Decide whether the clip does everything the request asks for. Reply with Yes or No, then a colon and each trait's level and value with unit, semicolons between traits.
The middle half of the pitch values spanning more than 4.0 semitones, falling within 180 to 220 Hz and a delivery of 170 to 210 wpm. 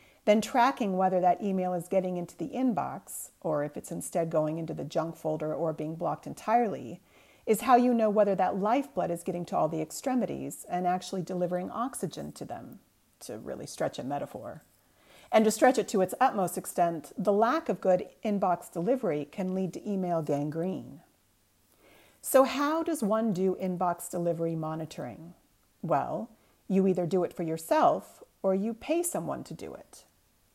Yes: average, 4.4 semitones; medium, 185 Hz; average, 175 wpm